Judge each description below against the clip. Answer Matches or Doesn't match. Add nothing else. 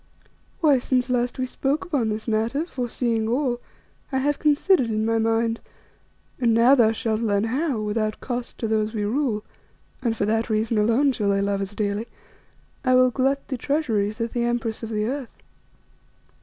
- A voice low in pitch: Doesn't match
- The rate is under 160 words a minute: Doesn't match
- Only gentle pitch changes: Doesn't match